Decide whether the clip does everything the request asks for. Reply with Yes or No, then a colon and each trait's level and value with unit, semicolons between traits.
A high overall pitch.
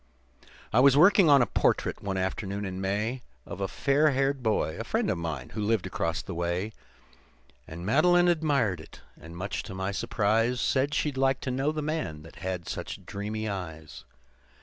No: low, 105 Hz